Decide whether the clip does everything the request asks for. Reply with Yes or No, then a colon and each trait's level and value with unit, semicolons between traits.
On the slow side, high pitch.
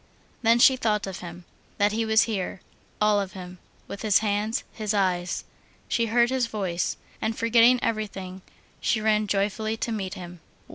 No: average, 170 wpm; high, 210 Hz